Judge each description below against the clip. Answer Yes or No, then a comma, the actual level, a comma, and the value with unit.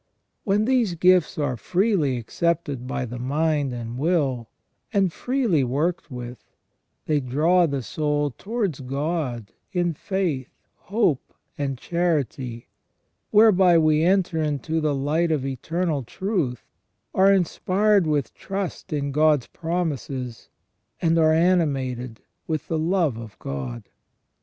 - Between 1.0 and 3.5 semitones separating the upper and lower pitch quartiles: No, average, 5.1 semitones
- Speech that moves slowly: Yes, slow, 125 wpm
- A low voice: No, medium, 155 Hz